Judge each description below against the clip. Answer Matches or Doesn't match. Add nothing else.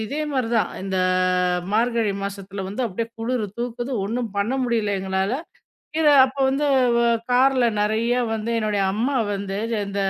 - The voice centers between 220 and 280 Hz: Matches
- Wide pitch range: Doesn't match